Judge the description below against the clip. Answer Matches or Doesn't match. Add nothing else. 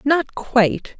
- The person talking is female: Matches